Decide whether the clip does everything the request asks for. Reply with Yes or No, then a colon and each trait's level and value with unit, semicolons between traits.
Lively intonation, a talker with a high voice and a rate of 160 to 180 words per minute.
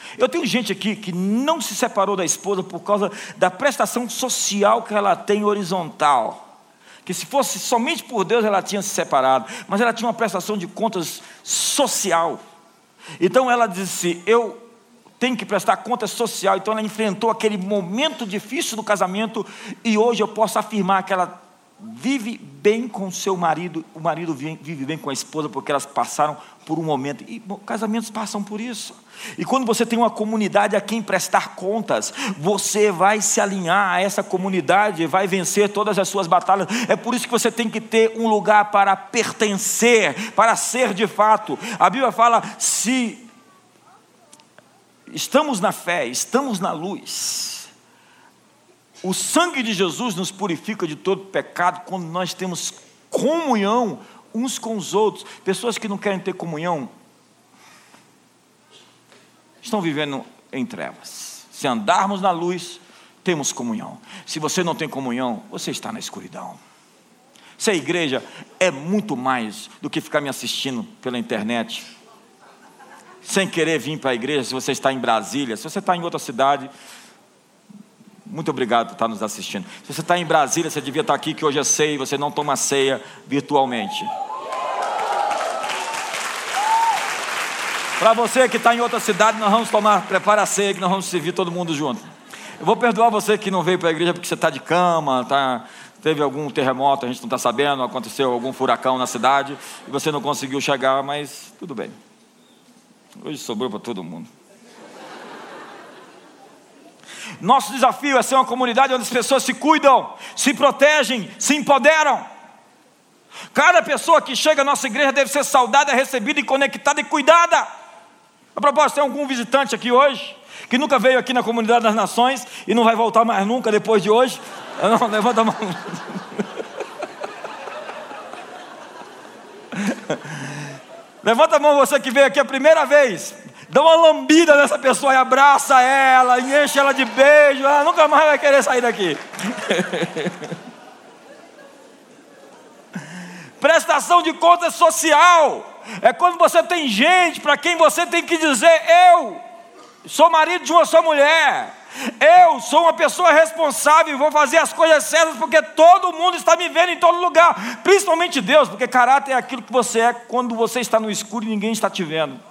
Yes: wide, 6.5 semitones; high, 220 Hz; average, 165 wpm